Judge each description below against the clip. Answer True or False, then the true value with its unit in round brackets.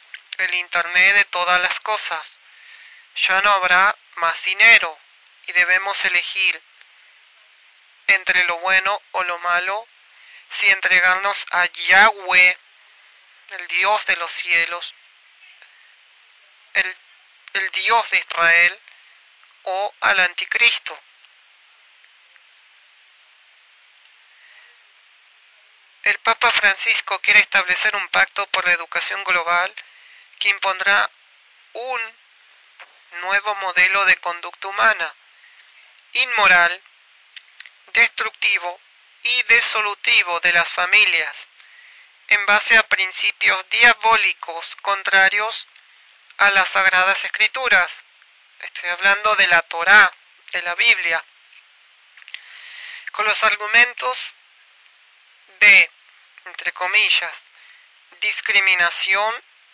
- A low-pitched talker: False (195 Hz)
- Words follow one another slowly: True (90 wpm)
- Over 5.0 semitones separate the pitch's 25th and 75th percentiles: False (3.5 semitones)